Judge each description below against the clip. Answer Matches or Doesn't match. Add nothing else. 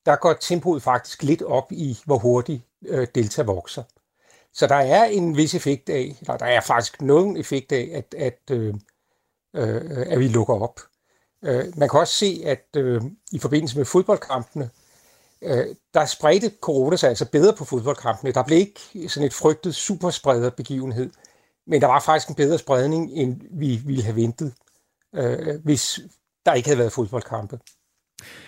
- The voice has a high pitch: Doesn't match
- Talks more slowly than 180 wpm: Matches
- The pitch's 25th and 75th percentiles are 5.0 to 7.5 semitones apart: Doesn't match